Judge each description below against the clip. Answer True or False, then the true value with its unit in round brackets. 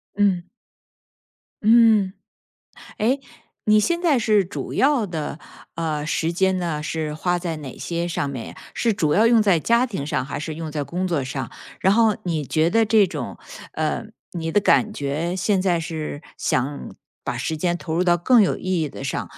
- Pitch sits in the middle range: True (175 Hz)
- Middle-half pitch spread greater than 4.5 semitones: True (5.0 semitones)